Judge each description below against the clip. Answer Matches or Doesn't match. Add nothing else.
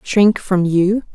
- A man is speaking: Doesn't match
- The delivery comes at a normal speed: Matches